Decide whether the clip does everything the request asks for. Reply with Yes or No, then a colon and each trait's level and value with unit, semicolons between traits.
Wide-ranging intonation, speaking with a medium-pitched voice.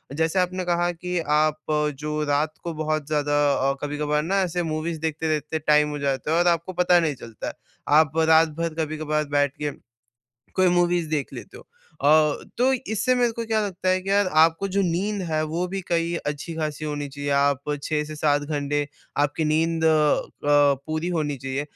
No: average, 2.9 semitones; medium, 155 Hz